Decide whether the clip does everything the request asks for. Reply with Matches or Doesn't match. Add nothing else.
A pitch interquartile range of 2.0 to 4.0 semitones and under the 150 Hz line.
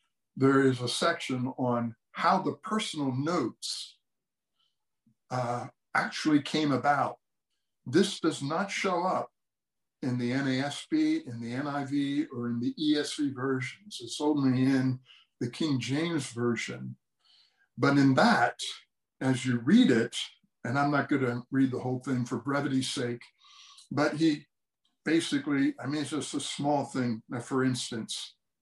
Matches